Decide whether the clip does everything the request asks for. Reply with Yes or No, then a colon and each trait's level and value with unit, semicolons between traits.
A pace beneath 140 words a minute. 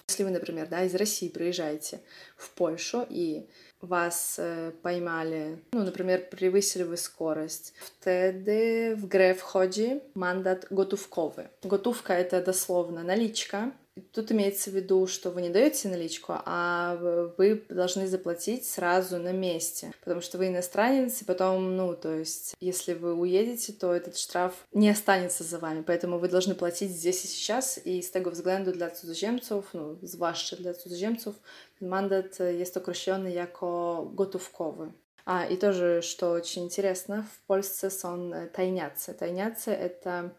No: average, 145 wpm